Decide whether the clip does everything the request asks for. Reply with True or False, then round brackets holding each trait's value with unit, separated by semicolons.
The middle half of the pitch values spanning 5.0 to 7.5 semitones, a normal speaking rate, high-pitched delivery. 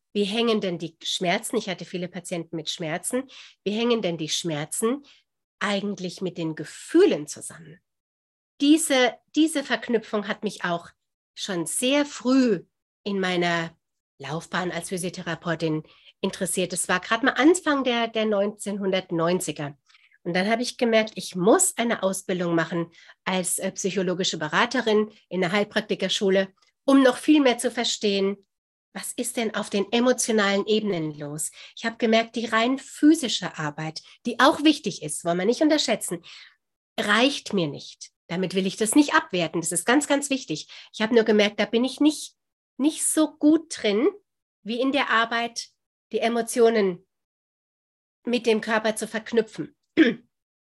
True (5.3 semitones; 150 wpm; 210 Hz)